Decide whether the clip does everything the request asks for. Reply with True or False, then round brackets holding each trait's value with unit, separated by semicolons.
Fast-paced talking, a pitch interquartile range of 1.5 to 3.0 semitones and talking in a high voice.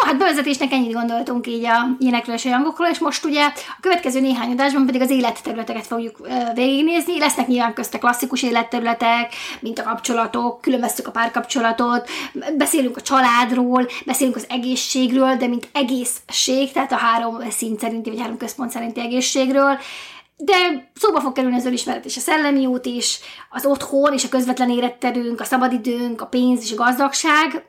True (170 wpm; 2.5 semitones; 250 Hz)